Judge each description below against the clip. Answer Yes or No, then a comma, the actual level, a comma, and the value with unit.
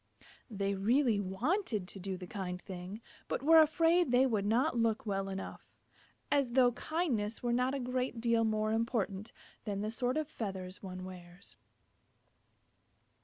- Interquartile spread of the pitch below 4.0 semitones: No, average, 4.6 semitones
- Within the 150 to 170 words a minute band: Yes, average, 155 wpm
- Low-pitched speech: No, high, 225 Hz